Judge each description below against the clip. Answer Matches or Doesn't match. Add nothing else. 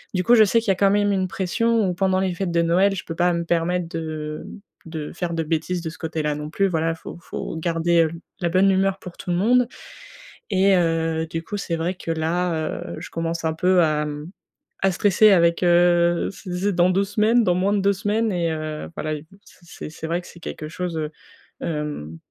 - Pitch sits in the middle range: Matches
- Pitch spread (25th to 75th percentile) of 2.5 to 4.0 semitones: Matches